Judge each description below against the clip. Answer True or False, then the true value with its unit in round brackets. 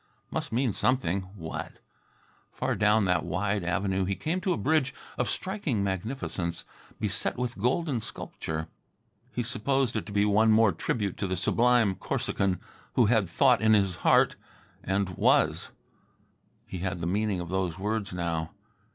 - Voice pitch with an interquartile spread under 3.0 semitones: False (4.7 semitones)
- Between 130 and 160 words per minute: True (155 wpm)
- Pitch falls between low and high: False (100 Hz)